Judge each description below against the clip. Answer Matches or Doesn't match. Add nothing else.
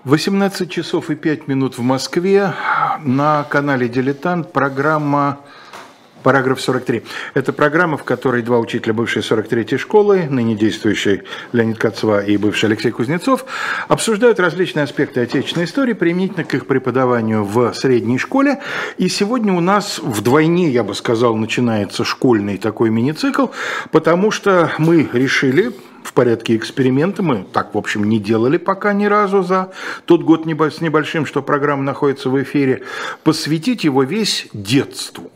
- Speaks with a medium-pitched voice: Matches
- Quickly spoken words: Doesn't match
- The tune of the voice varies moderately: Doesn't match